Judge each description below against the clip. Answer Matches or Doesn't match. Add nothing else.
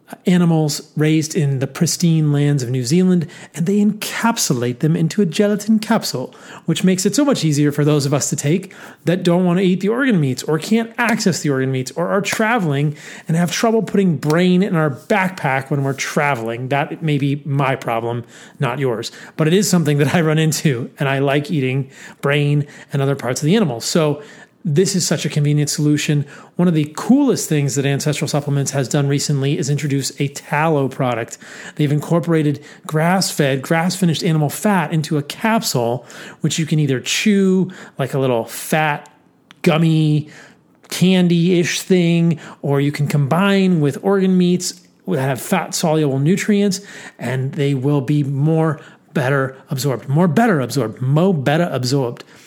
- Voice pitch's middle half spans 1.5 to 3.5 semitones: Doesn't match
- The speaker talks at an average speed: Matches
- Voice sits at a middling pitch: Matches